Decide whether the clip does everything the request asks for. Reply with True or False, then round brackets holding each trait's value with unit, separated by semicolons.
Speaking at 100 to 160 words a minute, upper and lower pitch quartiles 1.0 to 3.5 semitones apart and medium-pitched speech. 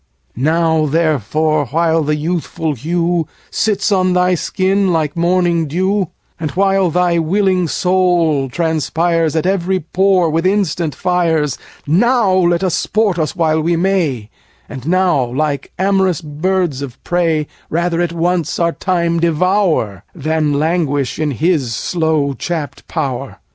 True (140 wpm; 2.9 semitones; 170 Hz)